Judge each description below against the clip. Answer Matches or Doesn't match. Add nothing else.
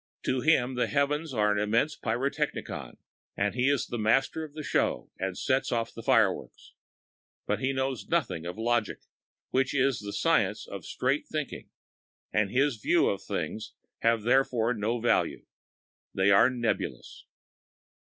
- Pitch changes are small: Doesn't match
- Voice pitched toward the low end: Matches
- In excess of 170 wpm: Doesn't match